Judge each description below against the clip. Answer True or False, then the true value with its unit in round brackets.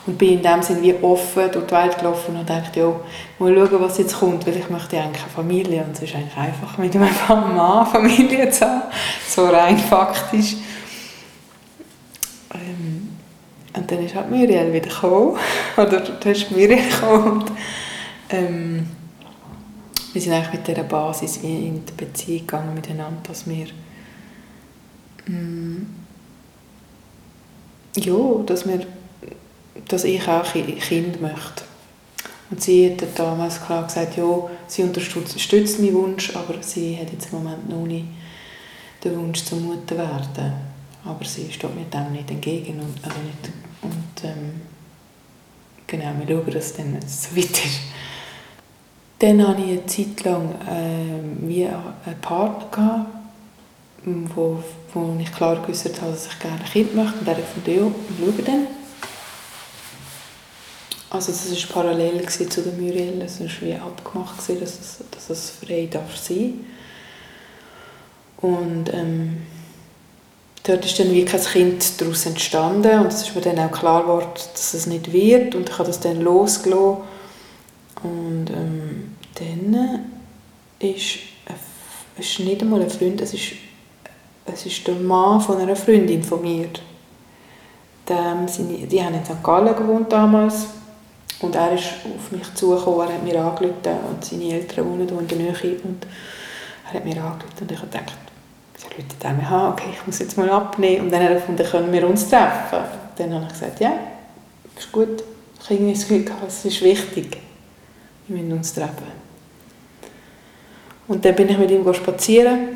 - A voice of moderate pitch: True (180 Hz)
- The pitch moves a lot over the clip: False (2.9 semitones)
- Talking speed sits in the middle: True (150 wpm)